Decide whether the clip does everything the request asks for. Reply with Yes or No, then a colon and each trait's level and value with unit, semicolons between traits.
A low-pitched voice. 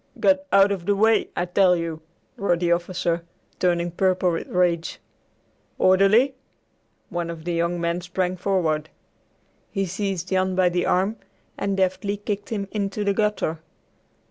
No: medium, 185 Hz